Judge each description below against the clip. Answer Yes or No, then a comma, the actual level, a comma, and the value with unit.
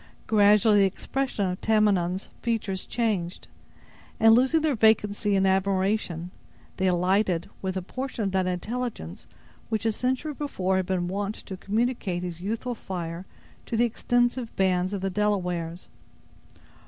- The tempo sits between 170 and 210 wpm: No, average, 140 wpm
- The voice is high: Yes, high, 200 Hz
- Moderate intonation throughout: Yes, average, 3.4 semitones